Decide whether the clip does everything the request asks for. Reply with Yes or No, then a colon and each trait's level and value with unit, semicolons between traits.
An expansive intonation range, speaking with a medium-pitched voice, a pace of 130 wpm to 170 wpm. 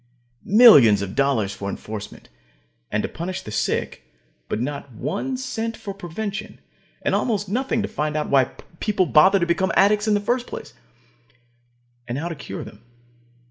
Yes: wide, 7.9 semitones; medium, 170 Hz; average, 155 wpm